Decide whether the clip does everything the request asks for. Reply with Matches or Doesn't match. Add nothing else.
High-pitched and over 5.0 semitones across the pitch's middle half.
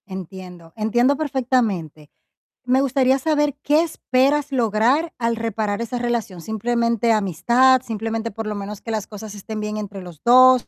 Doesn't match